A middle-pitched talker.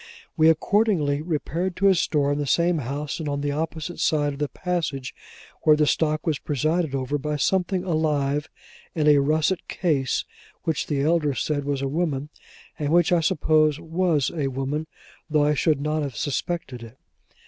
Yes: medium, 150 Hz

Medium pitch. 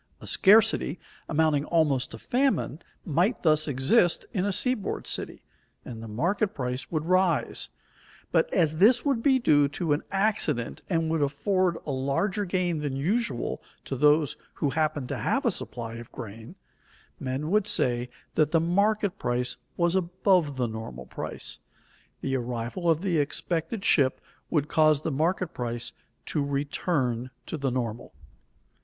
Yes: medium, 155 Hz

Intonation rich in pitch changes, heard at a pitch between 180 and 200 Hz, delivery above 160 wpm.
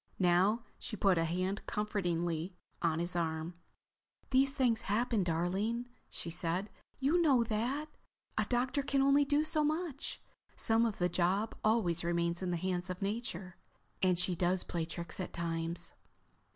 No: wide, 5.7 semitones; high, 190 Hz; average, 155 wpm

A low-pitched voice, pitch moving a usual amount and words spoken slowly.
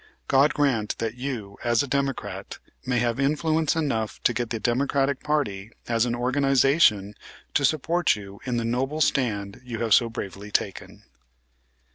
No: low, 125 Hz; average, 3.9 semitones; average, 155 wpm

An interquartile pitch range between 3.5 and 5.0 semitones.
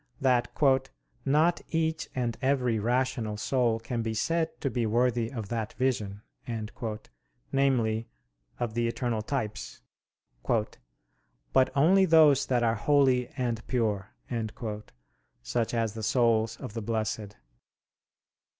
No: average, 3.0 semitones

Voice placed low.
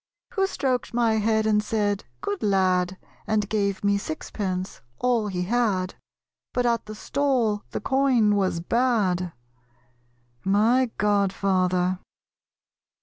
No: high, 210 Hz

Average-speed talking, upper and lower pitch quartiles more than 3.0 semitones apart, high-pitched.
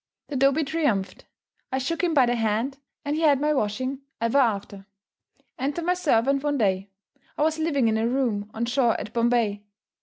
Yes: average, 185 wpm; average, 4.5 semitones; very high, 260 Hz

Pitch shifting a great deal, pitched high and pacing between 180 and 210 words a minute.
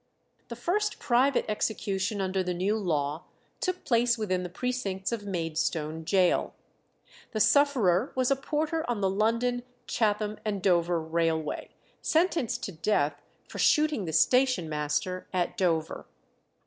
No: wide, 6.0 semitones; high, 200 Hz; slow, 135 wpm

